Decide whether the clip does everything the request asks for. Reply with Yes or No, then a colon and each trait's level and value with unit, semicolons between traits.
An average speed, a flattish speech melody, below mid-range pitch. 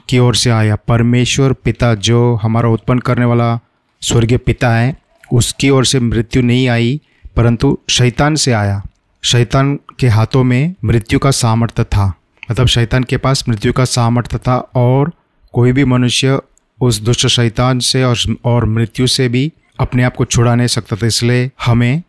Yes: average, 170 wpm; narrow, 1.7 semitones; low, 125 Hz